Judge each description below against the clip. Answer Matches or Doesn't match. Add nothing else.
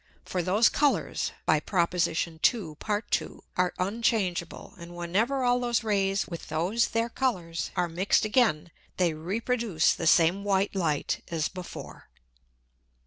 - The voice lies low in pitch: Doesn't match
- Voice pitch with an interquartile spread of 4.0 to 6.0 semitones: Matches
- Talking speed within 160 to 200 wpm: Doesn't match